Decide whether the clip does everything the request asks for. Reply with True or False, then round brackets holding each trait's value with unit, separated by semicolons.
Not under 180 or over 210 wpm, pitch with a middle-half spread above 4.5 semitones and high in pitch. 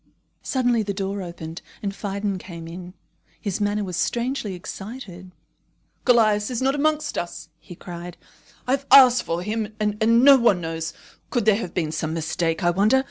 False (170 wpm; 5.2 semitones; 200 Hz)